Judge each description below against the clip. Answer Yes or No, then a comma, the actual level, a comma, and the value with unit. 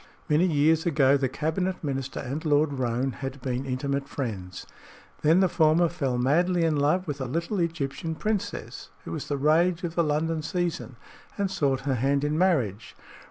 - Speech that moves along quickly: No, average, 175 wpm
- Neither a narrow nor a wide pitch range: Yes, average, 3.8 semitones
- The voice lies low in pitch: No, medium, 150 Hz